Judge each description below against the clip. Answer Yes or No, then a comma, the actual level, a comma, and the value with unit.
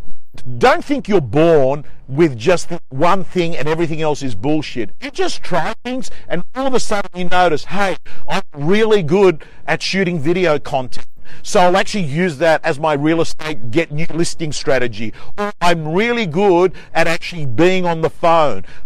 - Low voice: No, medium, 170 Hz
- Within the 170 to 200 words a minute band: Yes, average, 175 wpm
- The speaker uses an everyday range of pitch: Yes, average, 4.0 semitones